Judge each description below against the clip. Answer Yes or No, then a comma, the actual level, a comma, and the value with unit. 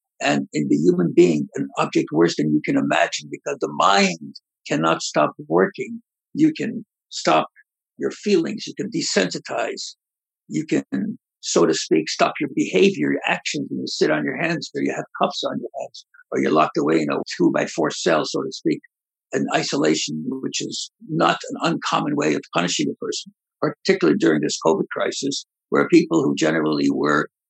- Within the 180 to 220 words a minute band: Yes, average, 185 wpm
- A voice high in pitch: Yes, very high, 275 Hz